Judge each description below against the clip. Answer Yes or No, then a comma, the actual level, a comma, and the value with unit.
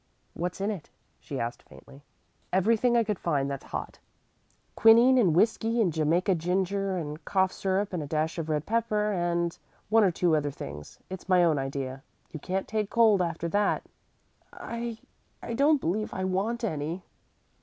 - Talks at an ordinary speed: Yes, average, 170 wpm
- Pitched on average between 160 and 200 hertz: Yes, medium, 185 Hz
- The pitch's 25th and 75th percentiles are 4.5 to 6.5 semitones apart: Yes, average, 5.1 semitones